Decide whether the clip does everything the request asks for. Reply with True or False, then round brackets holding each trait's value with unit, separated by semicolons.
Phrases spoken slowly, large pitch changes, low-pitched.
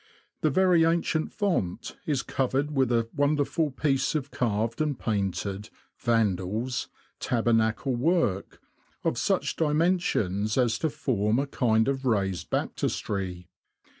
True (125 wpm; 5.8 semitones; 125 Hz)